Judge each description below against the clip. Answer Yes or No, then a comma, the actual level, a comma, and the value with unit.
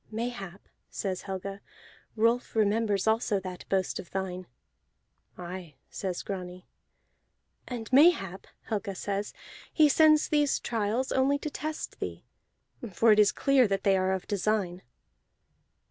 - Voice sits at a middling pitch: No, high, 205 Hz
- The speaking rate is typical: No, slow, 130 wpm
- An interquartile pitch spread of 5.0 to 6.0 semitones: No, average, 4.2 semitones